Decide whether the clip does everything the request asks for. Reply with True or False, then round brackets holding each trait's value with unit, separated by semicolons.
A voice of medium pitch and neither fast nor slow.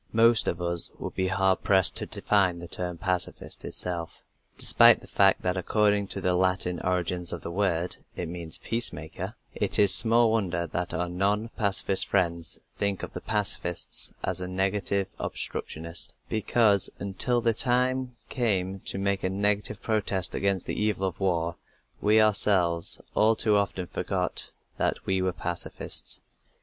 False (95 Hz; 160 wpm)